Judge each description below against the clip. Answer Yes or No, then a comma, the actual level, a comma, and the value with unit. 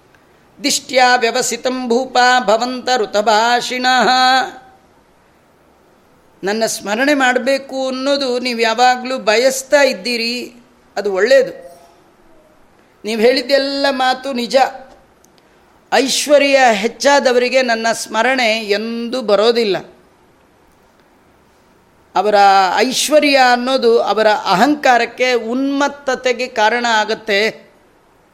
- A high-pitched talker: Yes, very high, 250 Hz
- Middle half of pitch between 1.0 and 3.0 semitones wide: Yes, average, 2.7 semitones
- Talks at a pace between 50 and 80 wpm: Yes, average, 70 wpm